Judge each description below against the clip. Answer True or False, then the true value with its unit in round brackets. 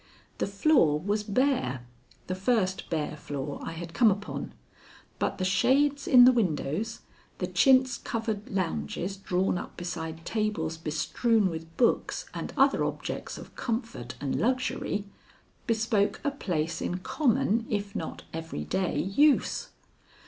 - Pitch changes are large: True (5.9 semitones)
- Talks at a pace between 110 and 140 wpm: True (135 wpm)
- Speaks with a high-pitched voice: True (195 Hz)